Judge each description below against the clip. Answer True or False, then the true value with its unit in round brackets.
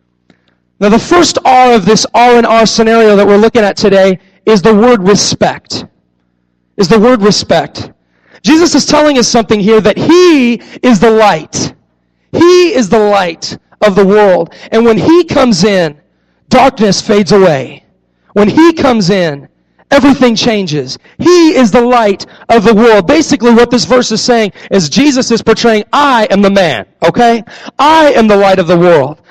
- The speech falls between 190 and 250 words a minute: False (170 wpm)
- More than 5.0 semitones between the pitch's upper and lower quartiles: False (4.1 semitones)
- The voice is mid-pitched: False (225 Hz)